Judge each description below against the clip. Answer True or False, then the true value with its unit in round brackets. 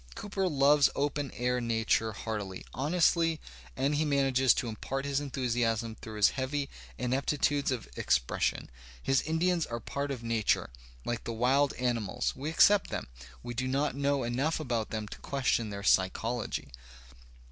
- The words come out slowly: False (155 wpm)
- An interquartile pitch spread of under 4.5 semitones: True (3.7 semitones)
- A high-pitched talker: False (130 Hz)